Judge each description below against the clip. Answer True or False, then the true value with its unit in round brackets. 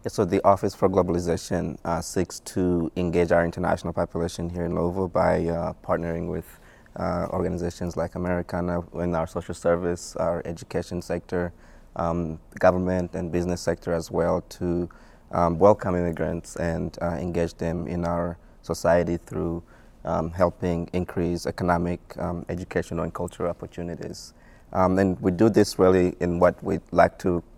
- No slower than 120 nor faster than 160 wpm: True (150 wpm)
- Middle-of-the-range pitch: False (85 Hz)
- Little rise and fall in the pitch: True (1.1 semitones)